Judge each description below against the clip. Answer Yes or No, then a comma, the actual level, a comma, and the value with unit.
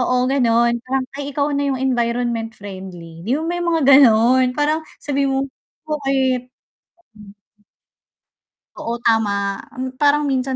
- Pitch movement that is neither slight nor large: Yes, average, 3.3 semitones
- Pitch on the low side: No, very high, 260 Hz